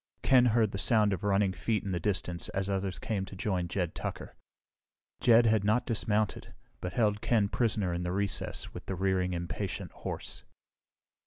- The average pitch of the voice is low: Yes, low, 100 Hz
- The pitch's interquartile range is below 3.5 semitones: Yes, average, 2.8 semitones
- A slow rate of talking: No, average, 175 wpm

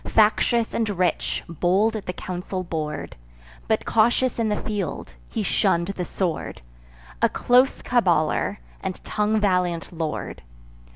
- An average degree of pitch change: Yes, average, 4.0 semitones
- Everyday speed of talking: No, slow, 130 wpm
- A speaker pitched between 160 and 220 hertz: Yes, high, 190 Hz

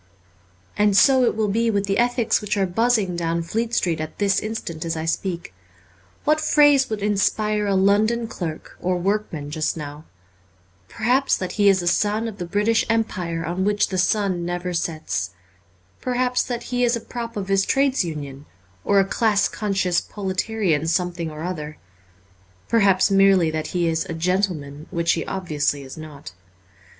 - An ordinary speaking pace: Yes, average, 170 wpm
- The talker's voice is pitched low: No, high, 195 Hz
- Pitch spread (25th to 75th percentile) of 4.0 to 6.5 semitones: Yes, average, 4.5 semitones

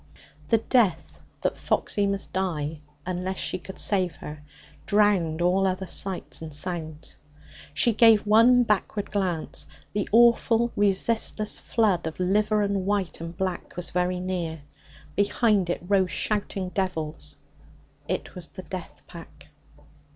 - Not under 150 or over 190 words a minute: No, slow, 135 wpm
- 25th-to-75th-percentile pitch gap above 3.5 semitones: No, average, 3.1 semitones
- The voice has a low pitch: No, high, 190 Hz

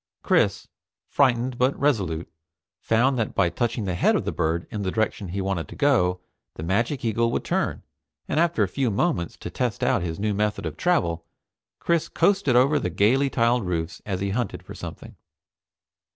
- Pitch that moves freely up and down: Yes, wide, 5.9 semitones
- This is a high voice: No, low, 110 Hz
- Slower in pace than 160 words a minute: No, average, 185 wpm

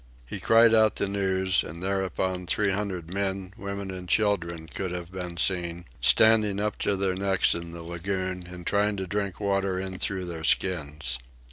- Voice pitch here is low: Yes, very low, 95 Hz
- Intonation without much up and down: Yes, narrow, 2.2 semitones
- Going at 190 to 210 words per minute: No, average, 175 wpm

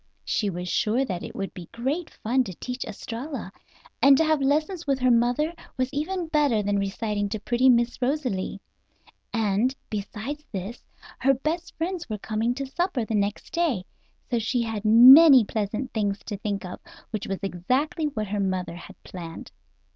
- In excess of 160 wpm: Yes, average, 175 wpm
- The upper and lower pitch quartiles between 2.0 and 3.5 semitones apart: No, average, 5.2 semitones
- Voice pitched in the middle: No, high, 235 Hz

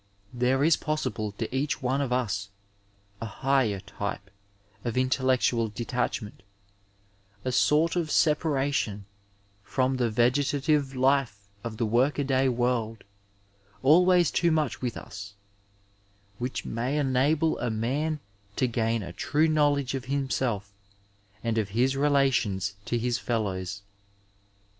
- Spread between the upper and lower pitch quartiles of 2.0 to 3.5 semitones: No, average, 4.3 semitones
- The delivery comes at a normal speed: No, slow, 130 wpm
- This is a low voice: Yes, low, 125 Hz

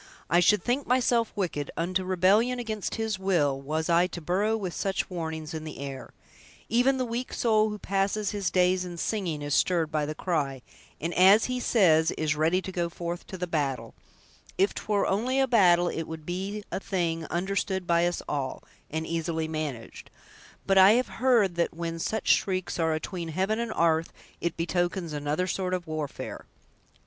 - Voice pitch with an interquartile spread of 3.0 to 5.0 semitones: Yes, average, 3.9 semitones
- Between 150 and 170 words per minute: No, average, 185 wpm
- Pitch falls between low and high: Yes, medium, 180 Hz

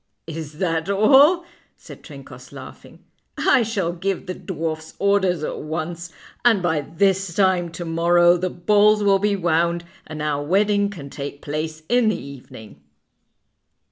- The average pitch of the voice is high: No, medium, 175 Hz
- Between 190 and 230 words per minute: No, average, 145 wpm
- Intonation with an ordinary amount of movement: Yes, average, 3.9 semitones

